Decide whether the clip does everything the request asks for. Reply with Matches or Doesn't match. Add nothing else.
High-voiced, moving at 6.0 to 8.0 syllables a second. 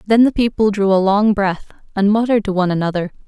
Matches